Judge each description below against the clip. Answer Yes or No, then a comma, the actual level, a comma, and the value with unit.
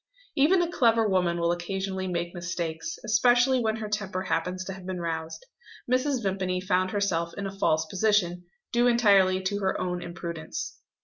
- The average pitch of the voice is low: No, high, 190 Hz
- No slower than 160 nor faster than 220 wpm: Yes, average, 170 wpm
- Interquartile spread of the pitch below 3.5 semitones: No, average, 3.9 semitones